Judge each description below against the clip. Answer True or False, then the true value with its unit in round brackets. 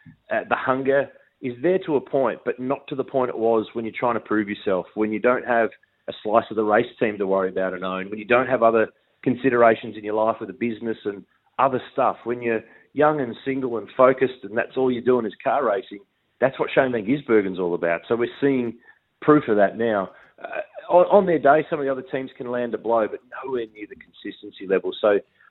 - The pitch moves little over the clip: False (3.6 semitones)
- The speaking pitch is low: True (120 Hz)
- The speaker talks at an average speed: False (240 wpm)